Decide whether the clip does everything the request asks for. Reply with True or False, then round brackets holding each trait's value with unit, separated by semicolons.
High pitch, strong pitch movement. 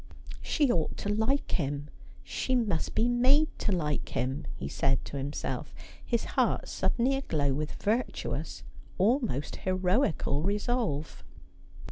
True (195 Hz; 8.6 semitones)